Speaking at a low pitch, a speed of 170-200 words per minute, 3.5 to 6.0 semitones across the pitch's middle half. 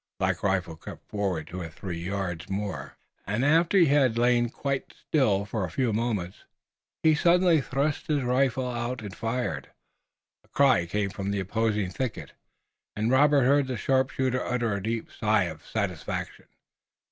No: low, 115 Hz; average, 160 wpm; average, 5.2 semitones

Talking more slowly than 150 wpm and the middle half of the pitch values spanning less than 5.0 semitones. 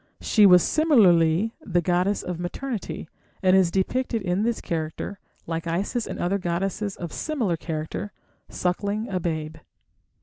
Yes: average, 140 wpm; average, 3.6 semitones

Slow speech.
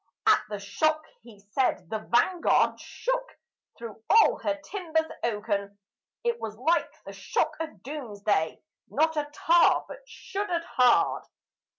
Yes: slow, 130 wpm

